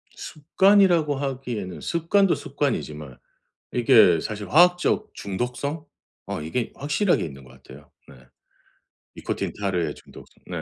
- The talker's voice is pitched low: Yes, low, 130 Hz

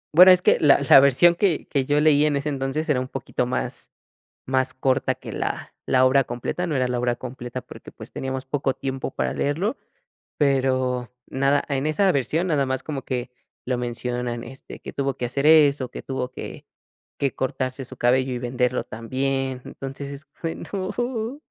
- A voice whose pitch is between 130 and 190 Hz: Yes, low, 135 Hz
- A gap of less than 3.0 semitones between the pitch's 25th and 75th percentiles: Yes, narrow, 2.4 semitones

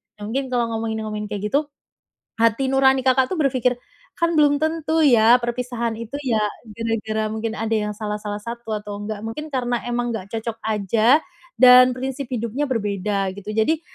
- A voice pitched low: No, high, 230 Hz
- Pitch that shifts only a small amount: No, average, 3.3 semitones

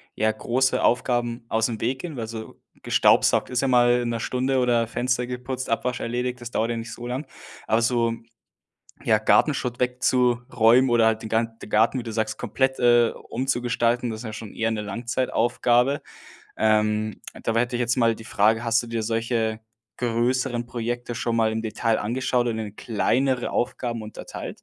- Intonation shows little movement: Yes, narrow, 1.7 semitones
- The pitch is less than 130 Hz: Yes, low, 120 Hz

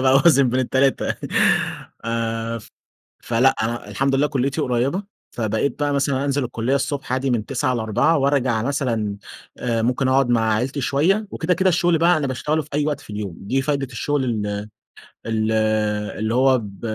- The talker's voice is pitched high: No, low, 130 Hz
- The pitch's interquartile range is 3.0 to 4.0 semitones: Yes, average, 3.5 semitones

